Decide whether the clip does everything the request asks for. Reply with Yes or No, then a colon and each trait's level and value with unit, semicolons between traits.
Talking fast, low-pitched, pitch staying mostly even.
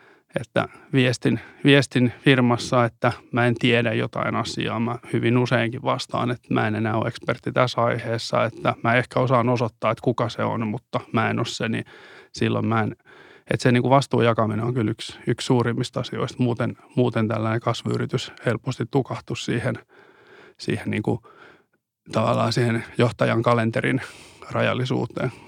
Yes: fast, 160 wpm; low, 120 Hz; narrow, 1.7 semitones